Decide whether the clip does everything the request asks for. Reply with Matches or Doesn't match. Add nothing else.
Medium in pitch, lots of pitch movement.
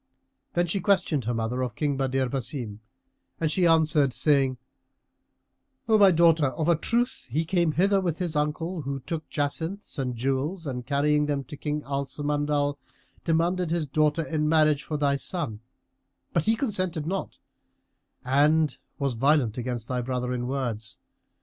Doesn't match